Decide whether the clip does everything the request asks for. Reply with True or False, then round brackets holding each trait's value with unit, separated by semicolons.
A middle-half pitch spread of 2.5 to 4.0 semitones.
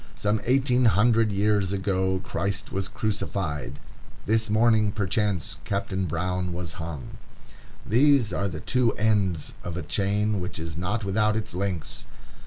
True (3.0 semitones)